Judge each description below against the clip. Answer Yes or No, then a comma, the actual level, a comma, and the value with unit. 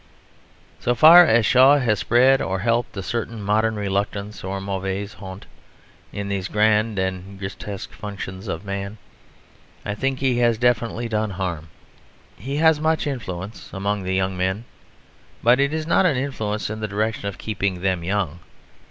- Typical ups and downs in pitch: Yes, average, 3.8 semitones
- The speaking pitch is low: Yes, low, 105 Hz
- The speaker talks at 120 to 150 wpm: No, average, 160 wpm